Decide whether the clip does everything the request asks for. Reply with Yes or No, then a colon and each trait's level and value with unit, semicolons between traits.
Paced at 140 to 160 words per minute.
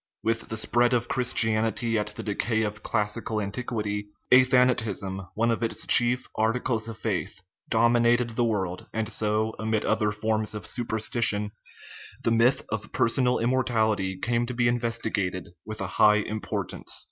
Yes: average, 155 wpm